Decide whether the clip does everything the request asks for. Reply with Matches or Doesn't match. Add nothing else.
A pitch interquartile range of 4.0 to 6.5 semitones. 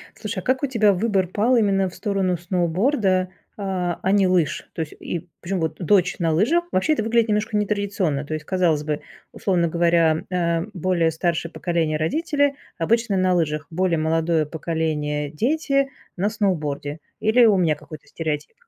Matches